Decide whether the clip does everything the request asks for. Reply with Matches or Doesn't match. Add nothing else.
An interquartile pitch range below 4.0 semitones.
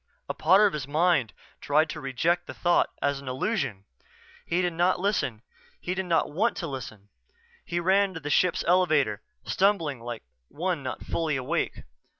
Doesn't match